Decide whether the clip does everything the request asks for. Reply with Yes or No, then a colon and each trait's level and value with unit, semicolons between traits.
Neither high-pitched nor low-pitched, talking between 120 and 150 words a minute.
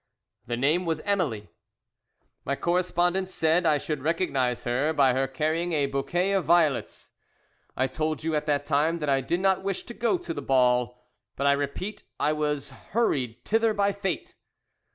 No: medium, 155 Hz; average, 175 wpm